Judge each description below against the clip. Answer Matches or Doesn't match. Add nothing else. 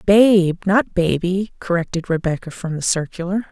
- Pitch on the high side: Doesn't match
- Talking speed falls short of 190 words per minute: Matches